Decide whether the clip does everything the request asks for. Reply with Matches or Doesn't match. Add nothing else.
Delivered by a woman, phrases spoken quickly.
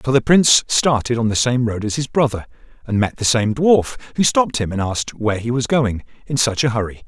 Doesn't match